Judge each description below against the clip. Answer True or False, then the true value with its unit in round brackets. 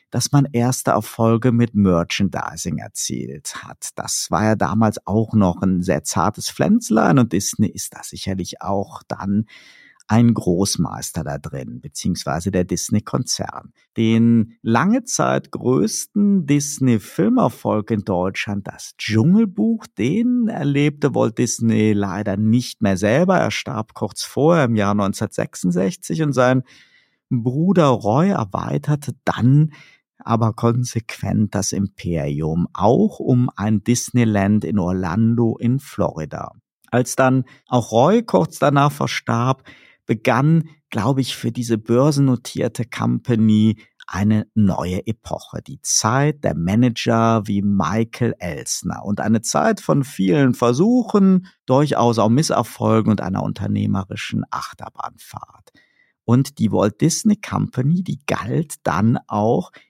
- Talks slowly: True (120 wpm)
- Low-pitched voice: True (115 Hz)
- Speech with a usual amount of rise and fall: True (5.0 semitones)